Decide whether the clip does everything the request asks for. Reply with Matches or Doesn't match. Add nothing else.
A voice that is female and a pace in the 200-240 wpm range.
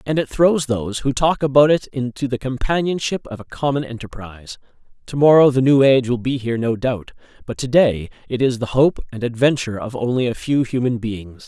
Doesn't match